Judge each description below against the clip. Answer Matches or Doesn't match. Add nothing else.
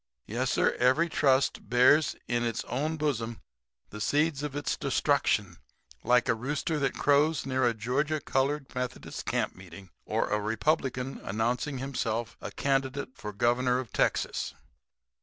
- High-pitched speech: Doesn't match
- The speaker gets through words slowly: Doesn't match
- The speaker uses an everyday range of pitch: Matches